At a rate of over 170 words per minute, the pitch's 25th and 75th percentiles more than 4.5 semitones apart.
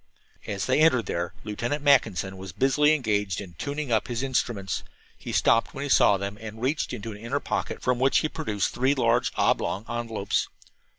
Yes: average, 185 wpm; average, 4.9 semitones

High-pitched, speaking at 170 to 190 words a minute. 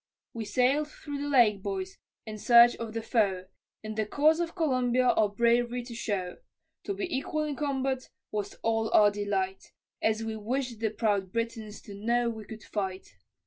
Yes: high, 225 Hz; average, 180 wpm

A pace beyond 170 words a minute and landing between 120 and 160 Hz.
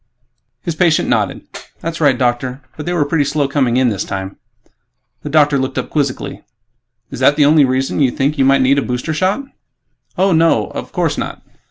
Yes: average, 195 wpm; medium, 140 Hz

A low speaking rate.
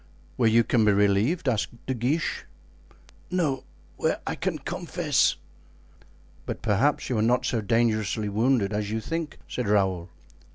No: average, 150 wpm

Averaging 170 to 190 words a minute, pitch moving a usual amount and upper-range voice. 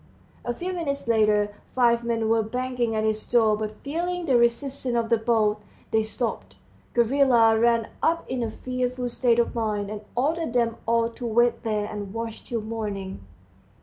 No: average, 175 wpm; narrow, 2.3 semitones; high, 230 Hz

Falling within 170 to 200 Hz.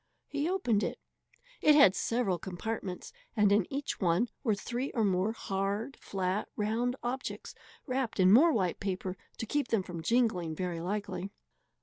No: high, 210 Hz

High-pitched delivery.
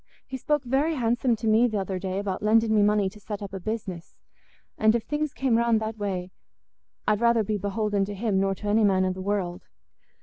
Yes: high, 210 Hz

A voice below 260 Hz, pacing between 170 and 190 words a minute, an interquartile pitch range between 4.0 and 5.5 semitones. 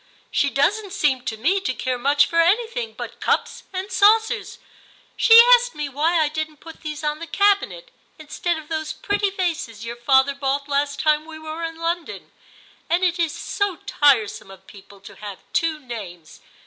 No: very high, 315 Hz; average, 185 wpm; average, 5.1 semitones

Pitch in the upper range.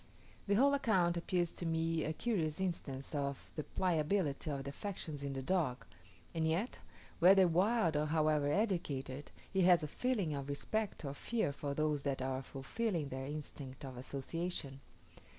No: medium, 155 Hz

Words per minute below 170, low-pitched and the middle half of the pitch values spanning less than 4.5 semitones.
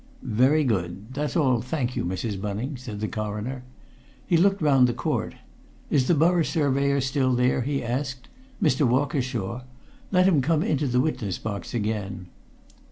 No: average, 160 wpm; low, 130 Hz; average, 4.8 semitones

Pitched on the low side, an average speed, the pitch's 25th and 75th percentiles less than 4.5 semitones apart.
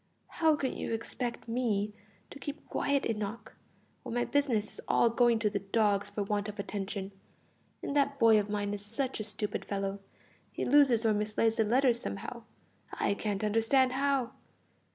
No: high, 225 Hz; average, 175 wpm; average, 3.5 semitones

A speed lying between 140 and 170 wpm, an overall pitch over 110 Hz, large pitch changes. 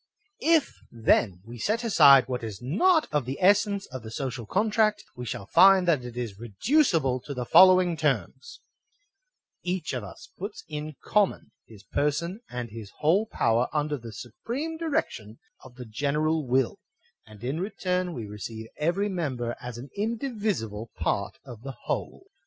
Yes: average, 165 wpm; medium, 140 Hz; wide, 8.3 semitones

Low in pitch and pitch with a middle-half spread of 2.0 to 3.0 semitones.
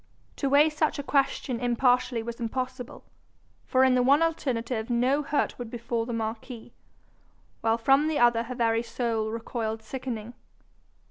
No: high, 245 Hz; narrow, 2.6 semitones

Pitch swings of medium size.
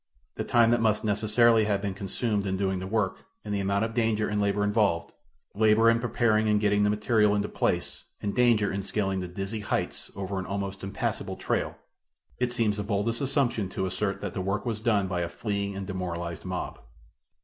No: narrow, 2.1 semitones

